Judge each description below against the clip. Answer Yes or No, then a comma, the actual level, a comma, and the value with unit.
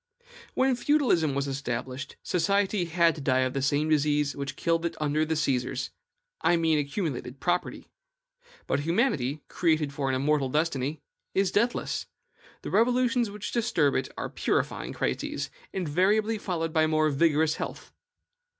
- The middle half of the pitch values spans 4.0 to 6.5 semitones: Yes, average, 4.6 semitones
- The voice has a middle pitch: Yes, medium, 155 Hz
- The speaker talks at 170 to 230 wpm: No, average, 145 wpm